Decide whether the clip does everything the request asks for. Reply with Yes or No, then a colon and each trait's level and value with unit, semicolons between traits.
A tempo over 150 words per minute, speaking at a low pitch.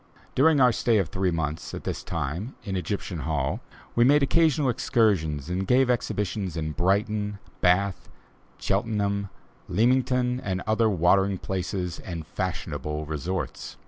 No: slow, 135 wpm; low, 100 Hz